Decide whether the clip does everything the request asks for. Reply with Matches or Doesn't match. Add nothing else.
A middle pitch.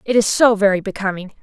Doesn't match